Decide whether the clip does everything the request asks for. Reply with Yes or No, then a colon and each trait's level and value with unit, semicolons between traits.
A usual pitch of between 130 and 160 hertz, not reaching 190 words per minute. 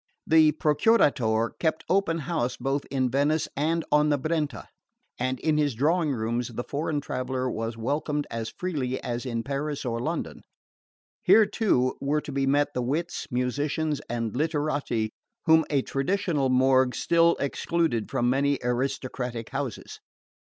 Yes: medium, 140 Hz; average, 145 wpm